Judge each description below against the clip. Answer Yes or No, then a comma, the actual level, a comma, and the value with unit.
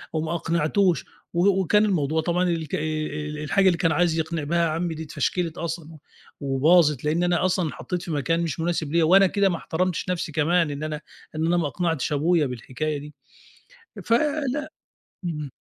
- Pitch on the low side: No, medium, 165 Hz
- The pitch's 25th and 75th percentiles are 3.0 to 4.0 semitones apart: No, narrow, 2.6 semitones